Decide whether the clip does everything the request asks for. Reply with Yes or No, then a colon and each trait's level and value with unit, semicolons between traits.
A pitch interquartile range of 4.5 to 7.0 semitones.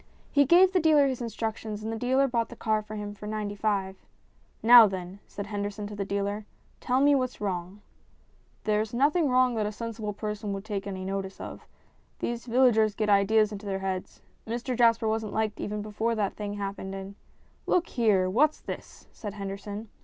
No: average, 2.7 semitones